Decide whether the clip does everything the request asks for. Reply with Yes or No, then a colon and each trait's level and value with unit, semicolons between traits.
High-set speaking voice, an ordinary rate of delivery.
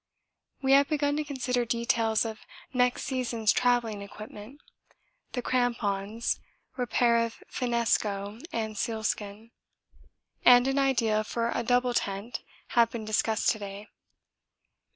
No: high, 235 Hz; slow, 120 wpm